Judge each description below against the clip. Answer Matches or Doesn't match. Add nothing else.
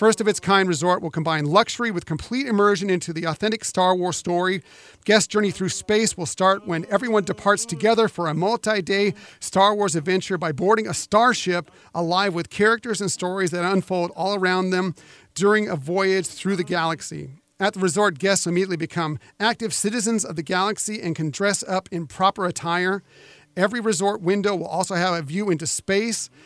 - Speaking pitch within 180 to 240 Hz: Matches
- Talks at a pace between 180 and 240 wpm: Matches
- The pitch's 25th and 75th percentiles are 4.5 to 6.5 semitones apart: Doesn't match